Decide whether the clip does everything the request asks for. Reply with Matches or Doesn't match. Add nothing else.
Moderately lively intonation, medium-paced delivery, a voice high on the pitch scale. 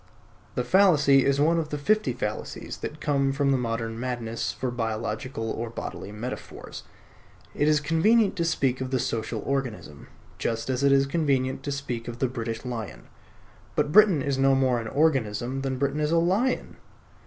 Doesn't match